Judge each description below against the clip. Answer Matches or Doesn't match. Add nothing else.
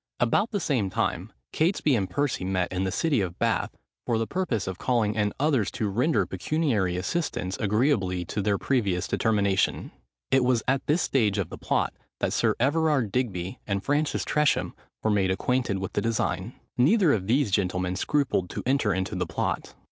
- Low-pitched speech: Matches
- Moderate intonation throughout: Doesn't match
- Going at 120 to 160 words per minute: Doesn't match